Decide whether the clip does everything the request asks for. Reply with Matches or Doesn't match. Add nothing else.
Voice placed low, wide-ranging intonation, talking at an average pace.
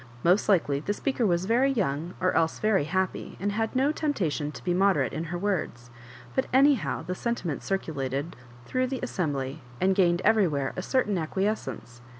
Doesn't match